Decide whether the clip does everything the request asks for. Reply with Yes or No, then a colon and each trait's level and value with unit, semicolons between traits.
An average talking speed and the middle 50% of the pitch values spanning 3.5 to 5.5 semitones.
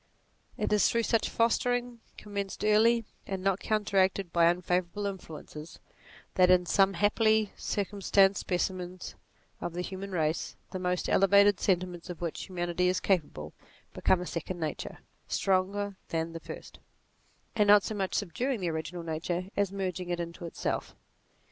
No: average, 150 wpm; narrow, 2.6 semitones